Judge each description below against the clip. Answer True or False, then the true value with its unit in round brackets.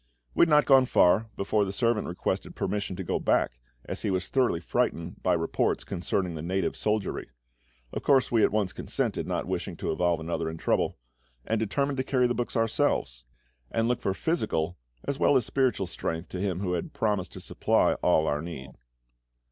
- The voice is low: True (95 Hz)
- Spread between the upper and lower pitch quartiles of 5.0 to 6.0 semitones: True (5.6 semitones)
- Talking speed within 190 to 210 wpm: True (195 wpm)